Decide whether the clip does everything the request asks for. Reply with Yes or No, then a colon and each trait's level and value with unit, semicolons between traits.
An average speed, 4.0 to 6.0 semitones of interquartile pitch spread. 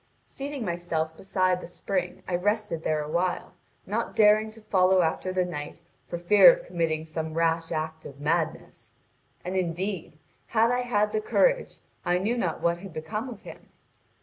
Yes: average, 170 wpm; average, 4.3 semitones